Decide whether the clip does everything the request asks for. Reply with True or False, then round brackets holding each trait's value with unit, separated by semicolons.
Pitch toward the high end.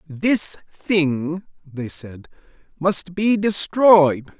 False (170 Hz)